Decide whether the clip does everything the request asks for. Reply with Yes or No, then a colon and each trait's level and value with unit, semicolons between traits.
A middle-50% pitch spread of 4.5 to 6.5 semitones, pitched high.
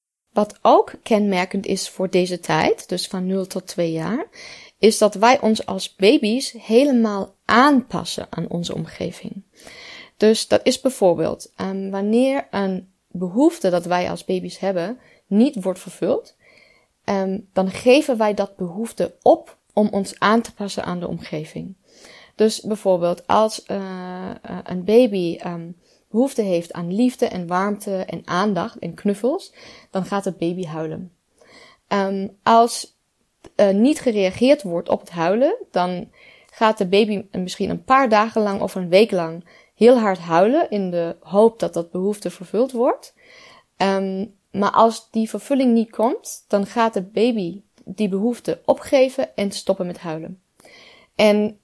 No: average, 3.7 semitones; high, 200 Hz